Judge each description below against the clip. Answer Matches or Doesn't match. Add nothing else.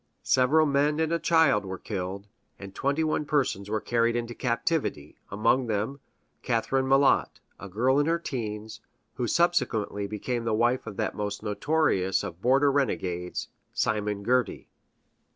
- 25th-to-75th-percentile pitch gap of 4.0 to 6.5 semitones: Matches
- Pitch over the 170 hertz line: Doesn't match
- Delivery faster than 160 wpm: Doesn't match